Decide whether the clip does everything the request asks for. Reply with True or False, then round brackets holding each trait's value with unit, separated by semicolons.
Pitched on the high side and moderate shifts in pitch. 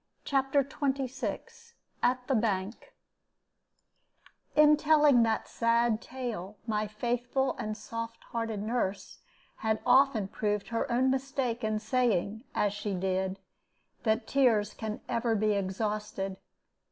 True (230 Hz; 3.5 semitones)